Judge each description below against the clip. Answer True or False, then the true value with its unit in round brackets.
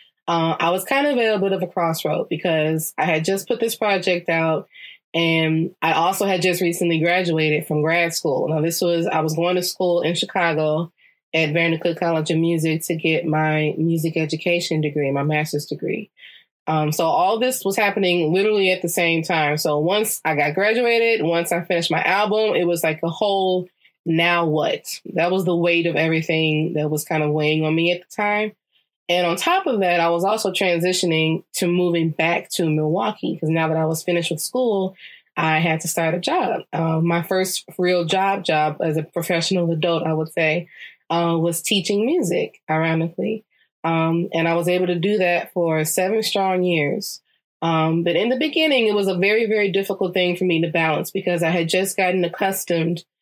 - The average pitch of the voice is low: False (170 Hz)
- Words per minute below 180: False (195 wpm)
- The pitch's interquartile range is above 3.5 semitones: False (2.7 semitones)